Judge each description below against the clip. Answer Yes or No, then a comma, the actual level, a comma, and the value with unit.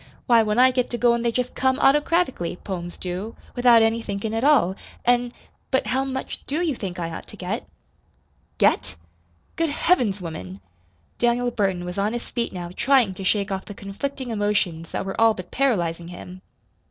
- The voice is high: Yes, high, 225 Hz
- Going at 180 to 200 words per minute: Yes, average, 185 wpm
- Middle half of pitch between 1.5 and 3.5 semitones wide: No, average, 5.0 semitones